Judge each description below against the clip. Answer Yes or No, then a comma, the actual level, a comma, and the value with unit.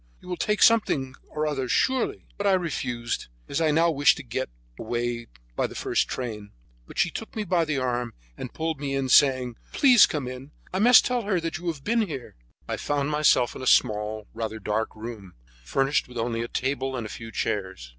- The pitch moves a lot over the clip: Yes, wide, 5.9 semitones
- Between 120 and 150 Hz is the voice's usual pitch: Yes, low, 135 Hz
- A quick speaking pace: Yes, fast, 215 wpm